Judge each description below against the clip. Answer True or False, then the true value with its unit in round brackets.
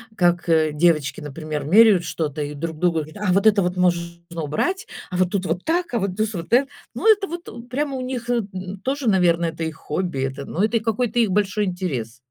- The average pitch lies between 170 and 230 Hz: True (185 Hz)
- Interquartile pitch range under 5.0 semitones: False (5.6 semitones)